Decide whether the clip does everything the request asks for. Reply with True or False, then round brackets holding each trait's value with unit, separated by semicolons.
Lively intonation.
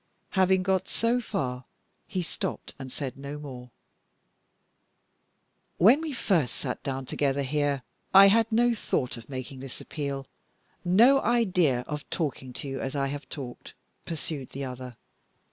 True (6.3 semitones)